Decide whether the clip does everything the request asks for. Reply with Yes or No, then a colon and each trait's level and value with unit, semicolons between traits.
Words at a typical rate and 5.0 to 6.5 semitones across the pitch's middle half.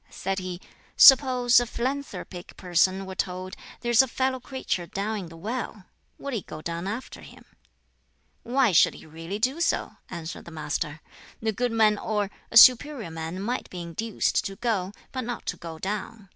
Yes: average, 175 wpm; average, 5.3 semitones